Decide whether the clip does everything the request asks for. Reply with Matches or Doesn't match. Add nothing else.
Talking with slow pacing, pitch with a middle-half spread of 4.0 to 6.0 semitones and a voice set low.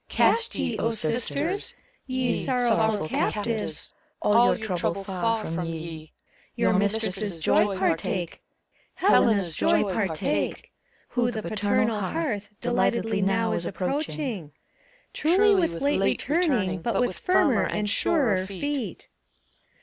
Doesn't match